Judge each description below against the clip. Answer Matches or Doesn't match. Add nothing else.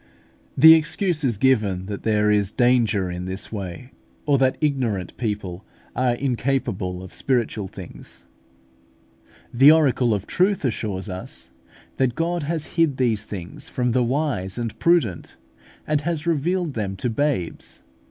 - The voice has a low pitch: Matches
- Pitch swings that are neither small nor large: Doesn't match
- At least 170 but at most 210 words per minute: Doesn't match